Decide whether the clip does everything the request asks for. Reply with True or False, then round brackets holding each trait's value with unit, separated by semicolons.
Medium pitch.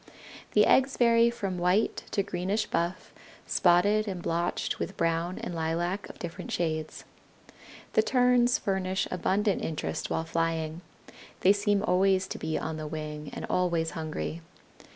True (180 Hz)